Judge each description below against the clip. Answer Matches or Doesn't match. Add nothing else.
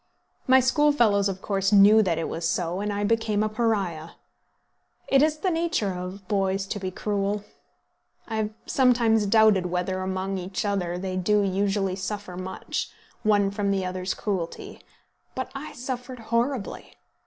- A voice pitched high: Matches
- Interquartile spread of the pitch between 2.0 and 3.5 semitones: Matches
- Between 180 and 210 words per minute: Doesn't match